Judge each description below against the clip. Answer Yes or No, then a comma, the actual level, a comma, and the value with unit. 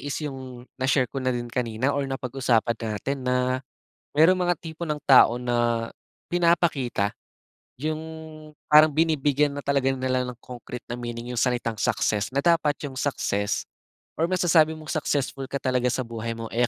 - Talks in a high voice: No, low, 130 Hz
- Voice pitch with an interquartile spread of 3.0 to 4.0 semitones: Yes, average, 3.6 semitones